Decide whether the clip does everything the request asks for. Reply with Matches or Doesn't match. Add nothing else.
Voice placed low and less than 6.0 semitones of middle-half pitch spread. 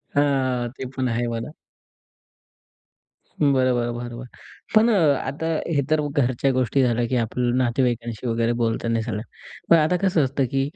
Matches